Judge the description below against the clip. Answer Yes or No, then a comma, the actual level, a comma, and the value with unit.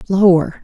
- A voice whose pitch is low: No, medium, 185 Hz